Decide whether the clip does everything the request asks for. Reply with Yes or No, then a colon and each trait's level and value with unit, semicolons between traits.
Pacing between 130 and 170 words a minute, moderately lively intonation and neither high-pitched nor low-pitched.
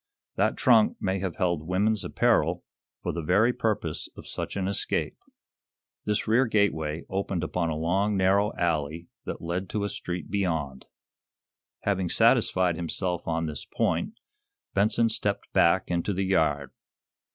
No: average, 145 wpm; average, 3.5 semitones; very low, 90 Hz